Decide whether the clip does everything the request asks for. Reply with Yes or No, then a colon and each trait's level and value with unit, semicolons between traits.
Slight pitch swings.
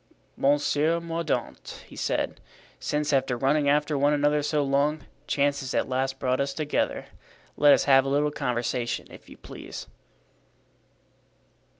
Yes: narrow, 1.7 semitones